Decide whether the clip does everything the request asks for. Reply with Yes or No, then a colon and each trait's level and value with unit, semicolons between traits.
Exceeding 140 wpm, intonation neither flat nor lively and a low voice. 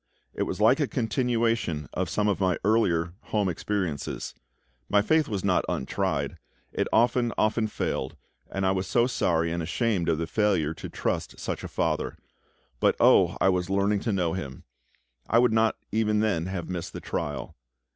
Yes: average, 175 wpm; average, 4.4 semitones; very low, 95 Hz